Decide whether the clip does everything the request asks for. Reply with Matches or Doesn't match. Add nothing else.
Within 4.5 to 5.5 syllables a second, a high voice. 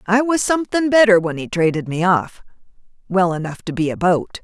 Doesn't match